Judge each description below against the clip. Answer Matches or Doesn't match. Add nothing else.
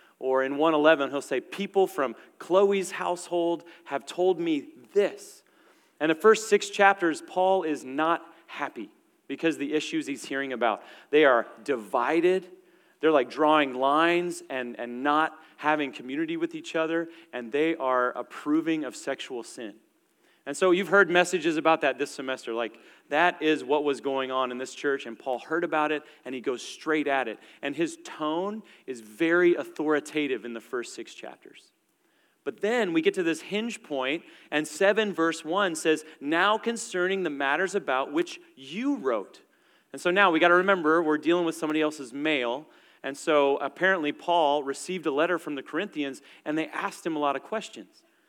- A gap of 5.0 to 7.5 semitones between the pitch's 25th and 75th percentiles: Matches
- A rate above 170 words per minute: Matches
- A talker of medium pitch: Matches